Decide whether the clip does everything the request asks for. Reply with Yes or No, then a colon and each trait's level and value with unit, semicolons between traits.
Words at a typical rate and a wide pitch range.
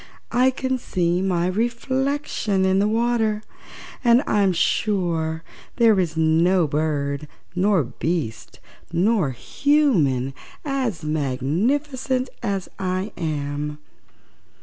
No: slow, 100 wpm; wide, 6.9 semitones